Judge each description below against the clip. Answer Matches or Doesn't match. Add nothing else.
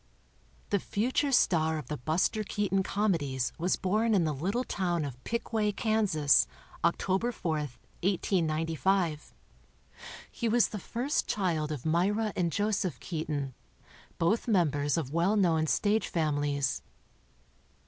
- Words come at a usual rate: Doesn't match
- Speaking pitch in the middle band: Matches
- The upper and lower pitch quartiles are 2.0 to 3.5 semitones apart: Doesn't match